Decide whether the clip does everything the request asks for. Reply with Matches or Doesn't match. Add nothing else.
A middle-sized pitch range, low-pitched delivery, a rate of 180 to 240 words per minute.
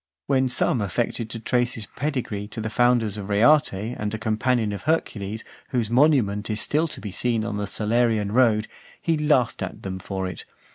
Matches